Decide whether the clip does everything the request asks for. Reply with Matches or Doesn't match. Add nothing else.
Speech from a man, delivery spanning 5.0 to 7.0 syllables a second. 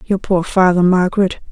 Doesn't match